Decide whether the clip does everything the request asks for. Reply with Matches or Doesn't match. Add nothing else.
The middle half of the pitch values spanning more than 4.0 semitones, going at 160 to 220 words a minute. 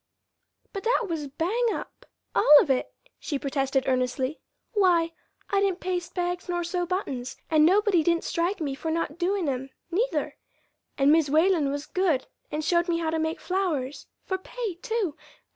Matches